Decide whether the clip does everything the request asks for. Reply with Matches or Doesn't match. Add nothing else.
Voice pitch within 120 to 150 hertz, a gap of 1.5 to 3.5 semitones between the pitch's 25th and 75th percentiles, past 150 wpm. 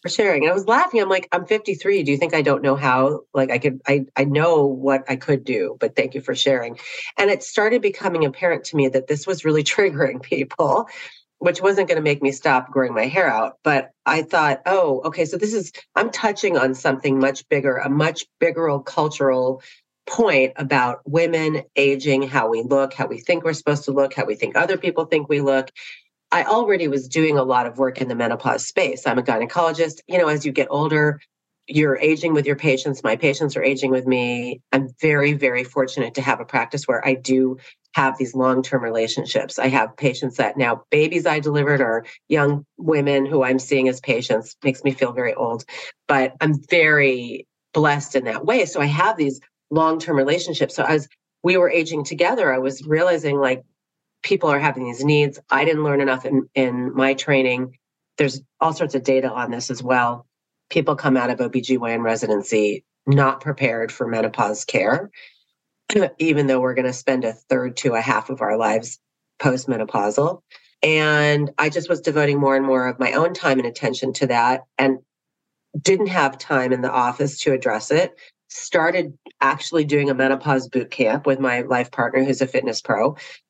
Matches